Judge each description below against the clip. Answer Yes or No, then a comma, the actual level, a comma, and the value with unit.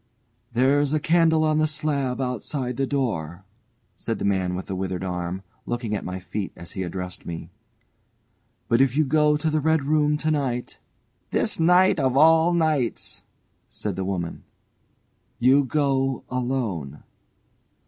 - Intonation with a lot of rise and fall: Yes, wide, 7.9 semitones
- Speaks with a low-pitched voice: Yes, low, 130 Hz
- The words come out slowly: No, average, 160 wpm